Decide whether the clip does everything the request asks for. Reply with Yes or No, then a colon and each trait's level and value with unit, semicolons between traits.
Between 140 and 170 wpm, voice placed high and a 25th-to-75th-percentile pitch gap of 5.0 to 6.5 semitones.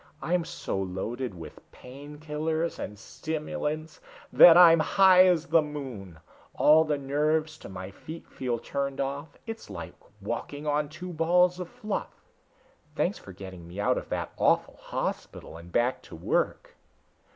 No: average, 150 wpm; medium, 150 Hz; wide, 5.4 semitones